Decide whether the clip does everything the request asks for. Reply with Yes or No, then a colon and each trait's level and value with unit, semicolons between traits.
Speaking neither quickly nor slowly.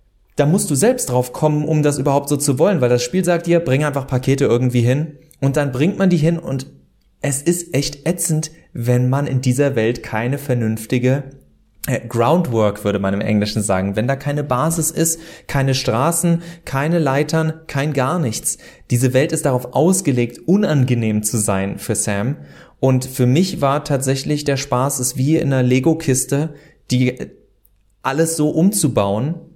Yes: average, 175 wpm